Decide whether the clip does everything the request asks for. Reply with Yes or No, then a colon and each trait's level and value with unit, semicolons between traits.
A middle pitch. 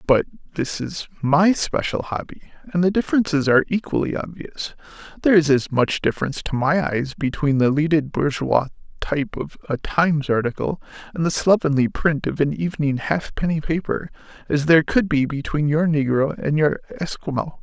Yes: medium, 155 Hz